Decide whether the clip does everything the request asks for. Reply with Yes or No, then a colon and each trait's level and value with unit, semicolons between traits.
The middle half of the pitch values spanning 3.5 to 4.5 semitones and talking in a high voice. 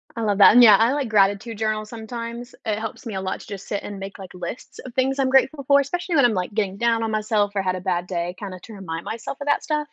Yes: average, 3.9 semitones; high, 220 Hz